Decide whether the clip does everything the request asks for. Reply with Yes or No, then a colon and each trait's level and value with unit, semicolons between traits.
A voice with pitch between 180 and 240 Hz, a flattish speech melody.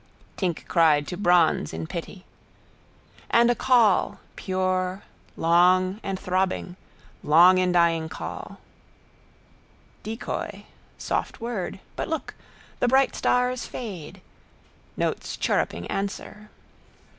No: medium, 185 Hz; average, 3.7 semitones